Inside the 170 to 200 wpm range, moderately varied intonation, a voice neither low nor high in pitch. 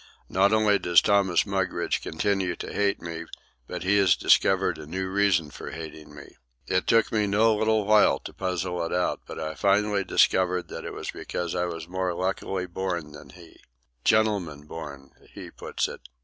No: average, 175 wpm; average, 3.4 semitones; very low, 90 Hz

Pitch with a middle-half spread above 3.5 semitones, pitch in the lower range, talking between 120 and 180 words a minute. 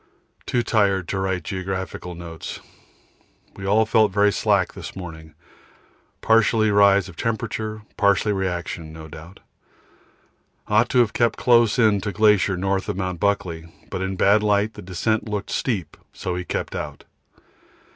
No: average, 2.9 semitones; low, 100 Hz; average, 150 wpm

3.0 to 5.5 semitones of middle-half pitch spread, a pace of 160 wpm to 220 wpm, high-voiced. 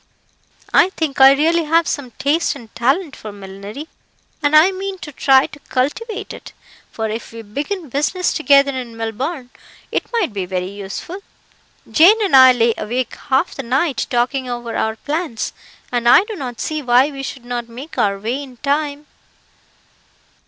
Yes: average, 4.9 semitones; average, 170 wpm; very high, 270 Hz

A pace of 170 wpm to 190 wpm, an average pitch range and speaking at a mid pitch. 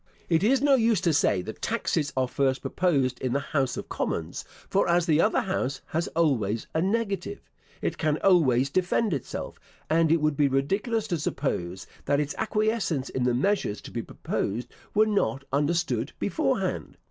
No: average, 180 wpm; wide, 6.7 semitones; medium, 155 Hz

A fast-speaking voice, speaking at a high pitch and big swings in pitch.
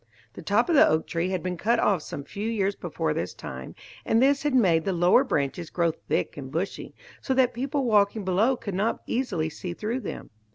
Yes: fast, 215 wpm; high, 200 Hz; wide, 6.0 semitones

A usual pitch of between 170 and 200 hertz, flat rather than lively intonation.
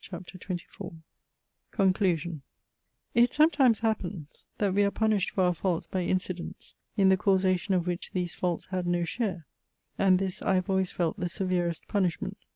Yes: medium, 185 Hz; narrow, 2.1 semitones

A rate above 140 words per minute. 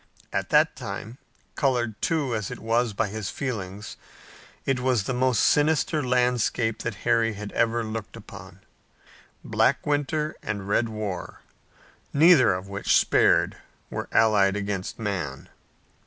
No: slow, 135 wpm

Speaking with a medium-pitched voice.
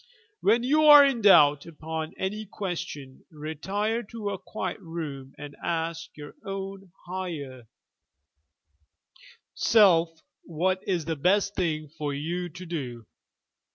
Yes: medium, 170 Hz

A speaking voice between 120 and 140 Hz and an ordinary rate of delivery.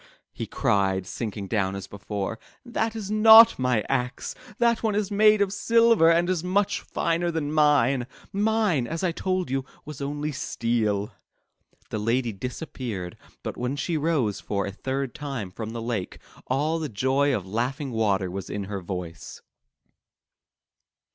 Yes: low, 135 Hz; average, 160 wpm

